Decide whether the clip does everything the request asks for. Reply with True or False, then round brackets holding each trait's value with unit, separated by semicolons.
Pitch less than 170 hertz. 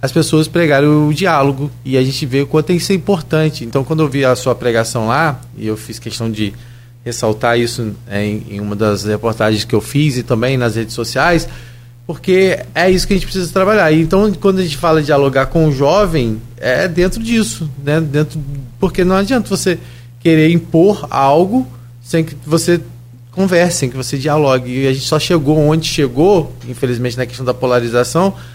True (140 Hz)